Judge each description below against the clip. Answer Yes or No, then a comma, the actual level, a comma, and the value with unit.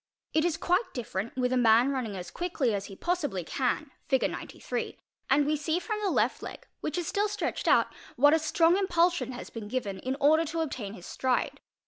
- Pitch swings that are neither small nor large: No, wide, 5.8 semitones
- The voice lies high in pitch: Yes, very high, 280 Hz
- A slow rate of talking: No, average, 195 wpm